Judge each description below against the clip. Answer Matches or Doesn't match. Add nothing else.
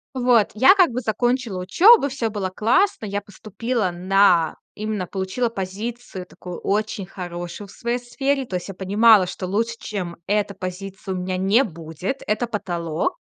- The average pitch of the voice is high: Matches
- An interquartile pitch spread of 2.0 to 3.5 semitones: Doesn't match